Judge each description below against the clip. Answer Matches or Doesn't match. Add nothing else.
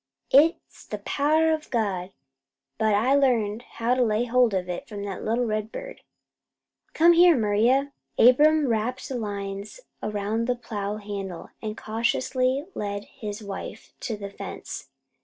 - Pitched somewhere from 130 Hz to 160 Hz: Doesn't match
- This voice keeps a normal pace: Matches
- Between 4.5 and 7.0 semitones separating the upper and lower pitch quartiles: Doesn't match